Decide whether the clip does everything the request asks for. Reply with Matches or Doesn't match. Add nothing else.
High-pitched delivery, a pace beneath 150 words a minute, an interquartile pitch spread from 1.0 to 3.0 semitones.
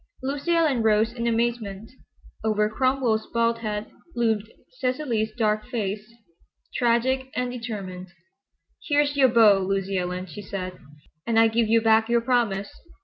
Matches